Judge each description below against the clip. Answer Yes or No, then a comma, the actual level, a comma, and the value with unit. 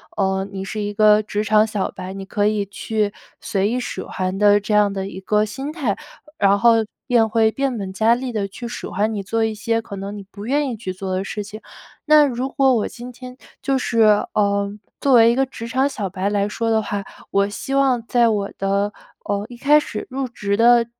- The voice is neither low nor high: No, high, 215 Hz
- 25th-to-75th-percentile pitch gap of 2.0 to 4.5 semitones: Yes, average, 3.1 semitones